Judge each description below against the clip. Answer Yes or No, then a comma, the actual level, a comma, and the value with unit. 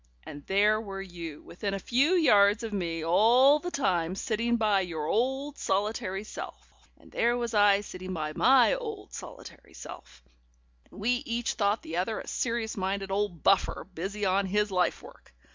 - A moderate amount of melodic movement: Yes, average, 4.1 semitones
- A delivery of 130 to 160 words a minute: No, average, 175 wpm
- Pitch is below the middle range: No, high, 205 Hz